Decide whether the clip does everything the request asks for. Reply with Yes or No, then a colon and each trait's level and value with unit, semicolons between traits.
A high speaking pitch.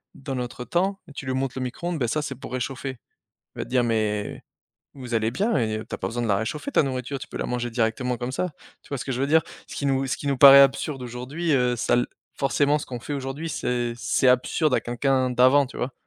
No: low, 130 Hz